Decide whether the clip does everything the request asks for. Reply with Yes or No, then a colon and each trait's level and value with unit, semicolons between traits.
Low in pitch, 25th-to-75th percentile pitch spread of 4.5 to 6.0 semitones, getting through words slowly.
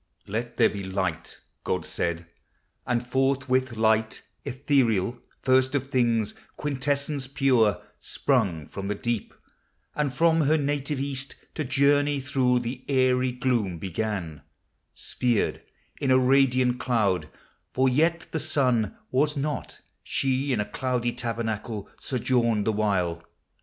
No: low, 125 Hz; average, 3.8 semitones; slow, 125 wpm